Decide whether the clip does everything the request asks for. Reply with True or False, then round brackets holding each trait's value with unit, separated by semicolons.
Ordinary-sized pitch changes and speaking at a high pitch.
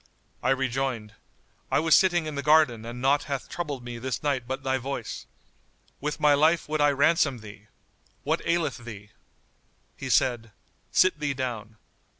False (3.8 semitones; 135 Hz)